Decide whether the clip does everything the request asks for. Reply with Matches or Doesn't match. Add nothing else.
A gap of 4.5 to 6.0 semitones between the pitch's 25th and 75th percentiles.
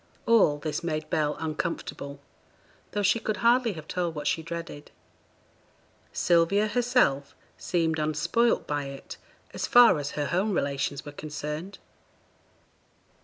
Matches